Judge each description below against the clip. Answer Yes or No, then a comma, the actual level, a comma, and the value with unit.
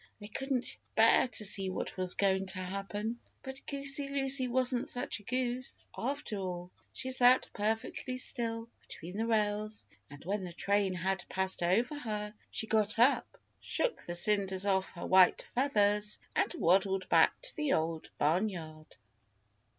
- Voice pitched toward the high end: Yes, high, 210 Hz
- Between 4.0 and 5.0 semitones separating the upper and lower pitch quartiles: Yes, average, 4.7 semitones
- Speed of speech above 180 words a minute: No, average, 155 wpm